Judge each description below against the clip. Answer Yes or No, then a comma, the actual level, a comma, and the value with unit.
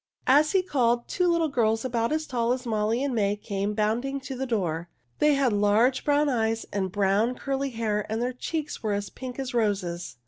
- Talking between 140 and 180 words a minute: No, fast, 205 wpm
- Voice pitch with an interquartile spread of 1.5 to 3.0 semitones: No, average, 4.4 semitones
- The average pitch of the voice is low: No, high, 235 Hz